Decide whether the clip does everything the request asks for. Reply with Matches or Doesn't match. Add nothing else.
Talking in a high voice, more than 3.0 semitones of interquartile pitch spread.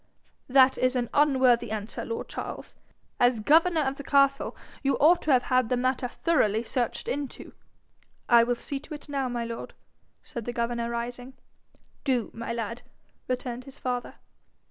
Doesn't match